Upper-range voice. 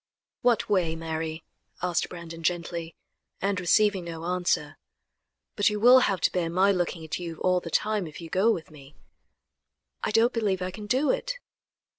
No: medium, 180 Hz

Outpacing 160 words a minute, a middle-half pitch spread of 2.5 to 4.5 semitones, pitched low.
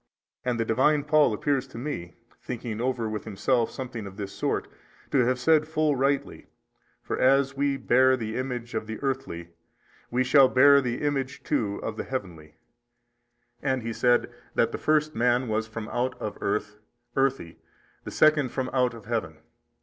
Yes: average, 170 wpm; average, 3.6 semitones; low, 125 Hz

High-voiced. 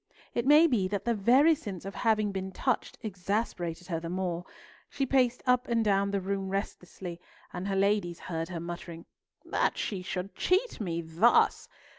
Yes: high, 195 Hz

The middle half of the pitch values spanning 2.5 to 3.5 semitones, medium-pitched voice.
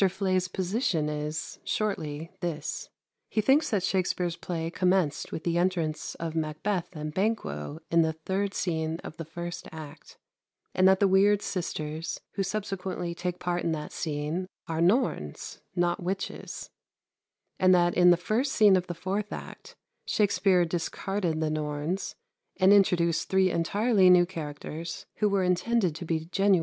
Yes: average, 3.1 semitones; medium, 175 Hz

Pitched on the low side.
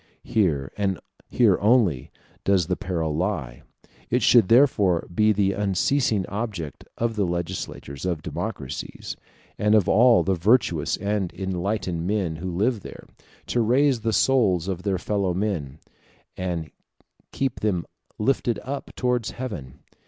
Yes: low, 100 Hz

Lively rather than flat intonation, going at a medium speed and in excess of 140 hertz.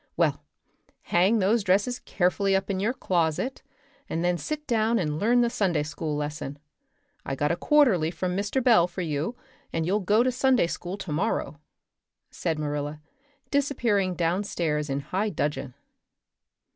Yes: wide, 6.1 semitones; average, 150 wpm; medium, 185 Hz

